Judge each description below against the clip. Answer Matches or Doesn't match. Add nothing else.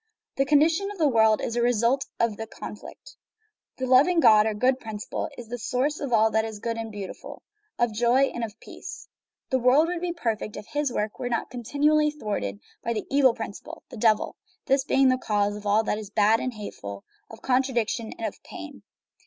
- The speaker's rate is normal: Doesn't match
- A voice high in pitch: Matches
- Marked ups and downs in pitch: Doesn't match